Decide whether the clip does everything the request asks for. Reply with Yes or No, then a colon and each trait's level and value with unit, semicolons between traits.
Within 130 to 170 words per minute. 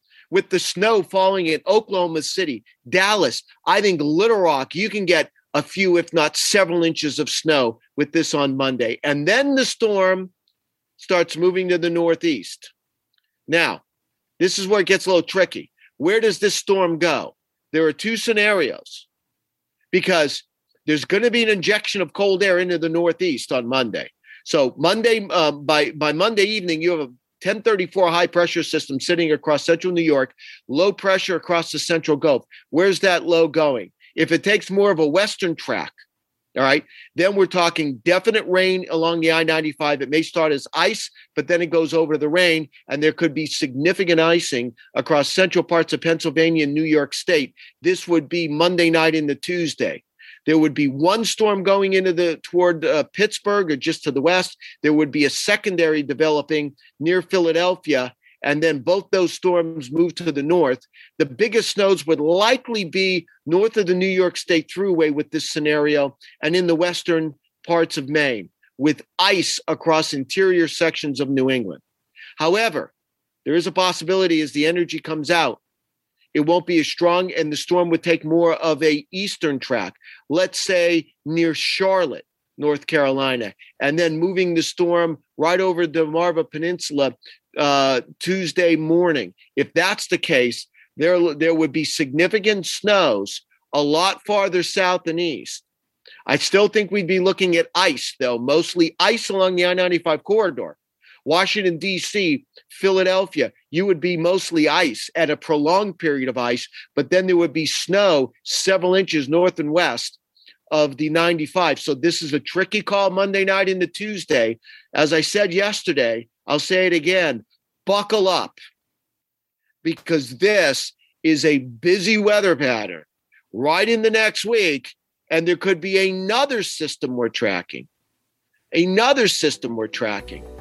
Yes: average, 165 wpm